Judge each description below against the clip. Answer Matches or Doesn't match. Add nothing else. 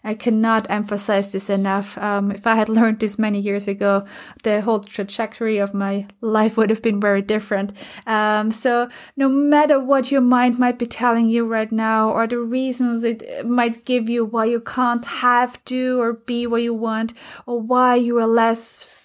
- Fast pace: Doesn't match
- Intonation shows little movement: Matches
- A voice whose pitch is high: Matches